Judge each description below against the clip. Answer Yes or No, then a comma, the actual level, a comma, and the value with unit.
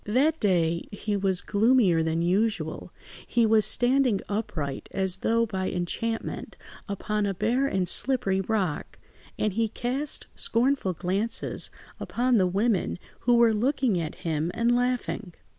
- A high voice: Yes, high, 210 Hz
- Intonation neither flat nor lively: Yes, average, 4.5 semitones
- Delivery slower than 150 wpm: Yes, average, 140 wpm